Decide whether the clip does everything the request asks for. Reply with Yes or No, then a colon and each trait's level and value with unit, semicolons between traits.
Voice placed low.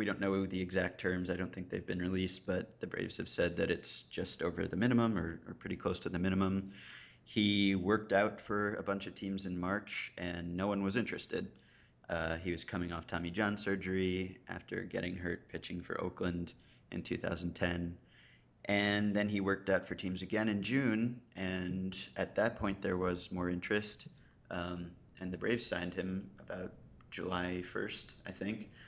Yes: very low, 95 Hz